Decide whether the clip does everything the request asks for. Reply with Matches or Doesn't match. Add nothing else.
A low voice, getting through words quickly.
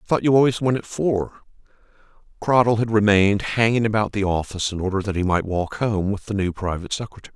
Matches